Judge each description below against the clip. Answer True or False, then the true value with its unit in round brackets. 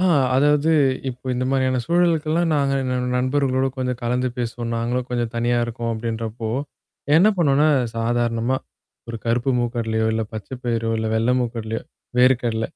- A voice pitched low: True (125 Hz)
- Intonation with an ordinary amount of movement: False (2.3 semitones)